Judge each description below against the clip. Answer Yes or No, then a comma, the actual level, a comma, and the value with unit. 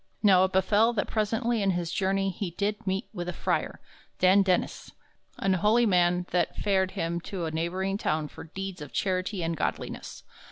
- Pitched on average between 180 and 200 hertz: Yes, high, 190 Hz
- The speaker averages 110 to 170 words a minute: No, average, 185 wpm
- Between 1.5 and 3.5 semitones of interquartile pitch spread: Yes, narrow, 2.5 semitones